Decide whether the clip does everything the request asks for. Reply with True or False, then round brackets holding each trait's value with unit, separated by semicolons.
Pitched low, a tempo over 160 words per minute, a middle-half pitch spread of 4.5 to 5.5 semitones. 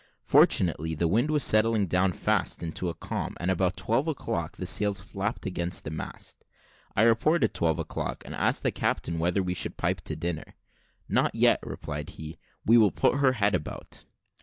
True (95 Hz; 185 wpm; 4.9 semitones)